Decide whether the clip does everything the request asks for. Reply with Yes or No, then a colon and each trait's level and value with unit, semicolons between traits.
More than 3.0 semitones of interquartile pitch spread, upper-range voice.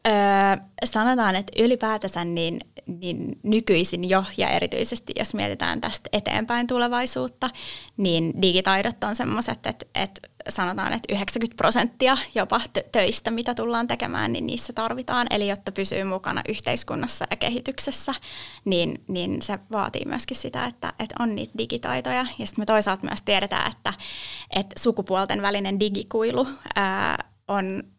Yes: average, 3.8 semitones; high, 215 Hz